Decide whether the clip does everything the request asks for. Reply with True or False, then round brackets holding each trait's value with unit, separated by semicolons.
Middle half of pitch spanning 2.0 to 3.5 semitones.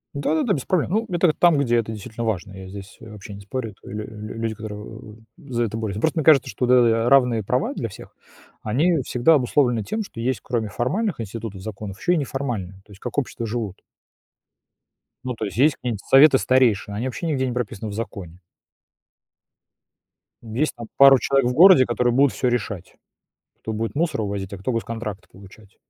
False (4.2 semitones)